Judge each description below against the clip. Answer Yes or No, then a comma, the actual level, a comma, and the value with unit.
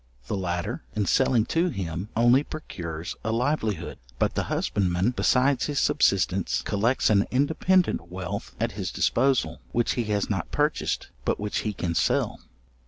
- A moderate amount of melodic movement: No, wide, 5.9 semitones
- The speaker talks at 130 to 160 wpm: Yes, average, 155 wpm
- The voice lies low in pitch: Yes, low, 110 Hz